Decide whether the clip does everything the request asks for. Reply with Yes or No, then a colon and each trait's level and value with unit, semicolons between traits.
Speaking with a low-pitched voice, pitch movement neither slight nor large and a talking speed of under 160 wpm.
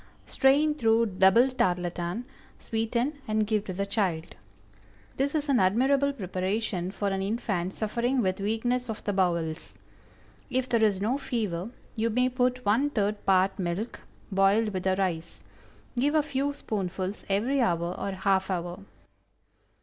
No: high, 210 Hz; average, 4.7 semitones; average, 150 wpm